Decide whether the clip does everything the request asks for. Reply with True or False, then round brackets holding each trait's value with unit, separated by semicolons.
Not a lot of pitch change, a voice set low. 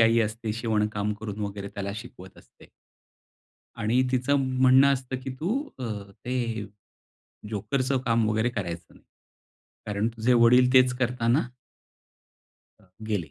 False (3.2 semitones; 115 Hz)